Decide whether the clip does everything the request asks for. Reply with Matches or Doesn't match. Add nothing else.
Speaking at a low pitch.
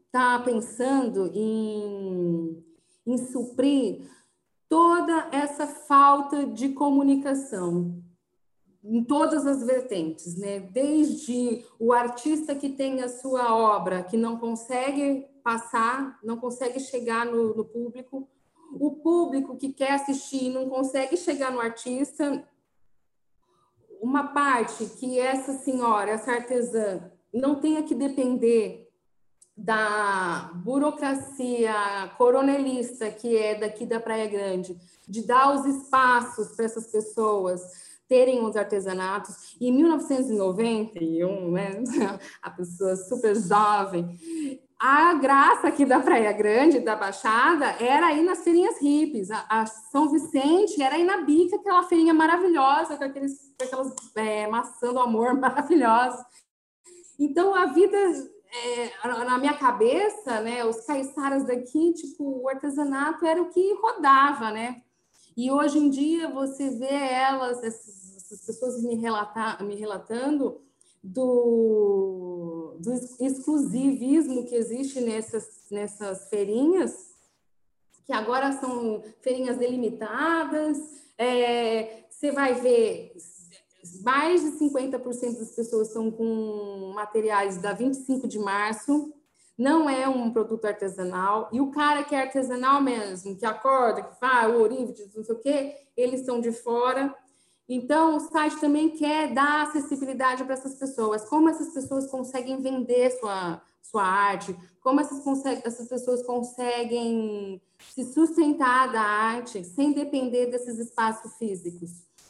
Doesn't match